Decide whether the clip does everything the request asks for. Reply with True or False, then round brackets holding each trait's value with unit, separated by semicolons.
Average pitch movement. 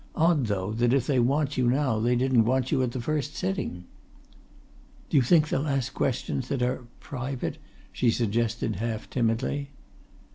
True (3.0 semitones)